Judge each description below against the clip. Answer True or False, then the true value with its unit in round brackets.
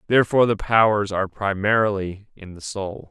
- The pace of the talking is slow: False (155 wpm)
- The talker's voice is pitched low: True (105 Hz)